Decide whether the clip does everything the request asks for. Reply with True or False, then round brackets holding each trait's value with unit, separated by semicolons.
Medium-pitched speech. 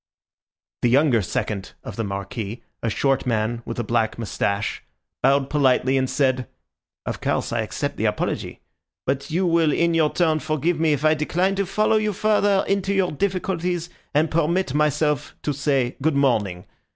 True (150 Hz)